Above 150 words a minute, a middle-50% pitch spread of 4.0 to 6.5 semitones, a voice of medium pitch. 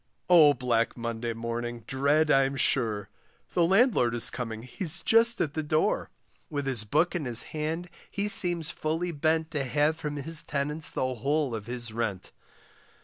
Yes: average, 165 wpm; average, 5.0 semitones; medium, 145 Hz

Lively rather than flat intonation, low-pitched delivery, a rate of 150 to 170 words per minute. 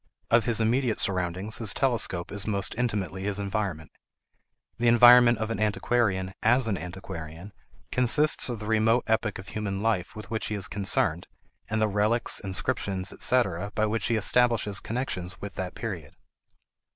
No: average, 3.3 semitones; low, 105 Hz; average, 160 wpm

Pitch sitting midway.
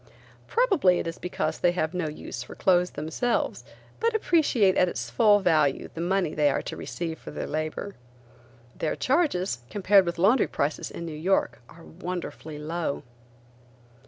Yes: medium, 175 Hz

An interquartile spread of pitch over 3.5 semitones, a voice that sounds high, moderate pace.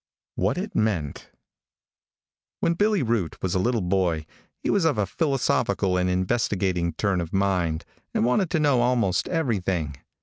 No: wide, 5.6 semitones; low, 100 Hz; average, 155 wpm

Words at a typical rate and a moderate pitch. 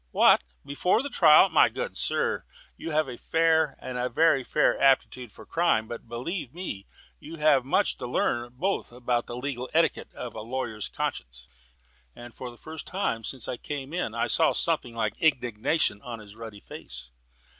No: average, 175 wpm; low, 125 Hz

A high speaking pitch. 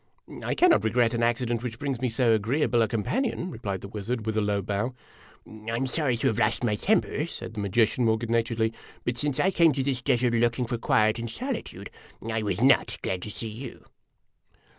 No: low, 115 Hz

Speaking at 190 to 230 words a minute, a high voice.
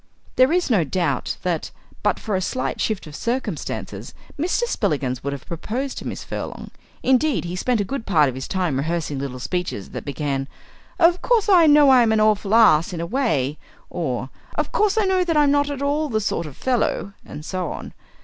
Yes: fast, 205 wpm; high, 205 Hz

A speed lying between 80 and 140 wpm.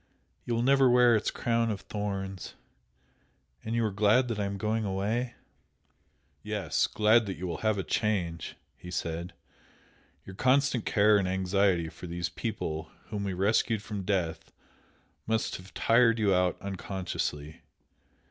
No: average, 150 wpm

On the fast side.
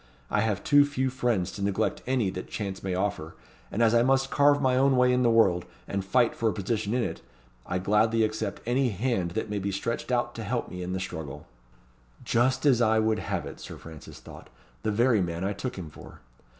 Yes: fast, 225 wpm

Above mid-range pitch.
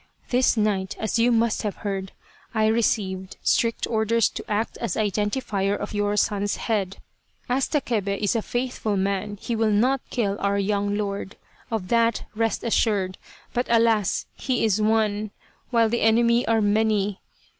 Yes: high, 215 Hz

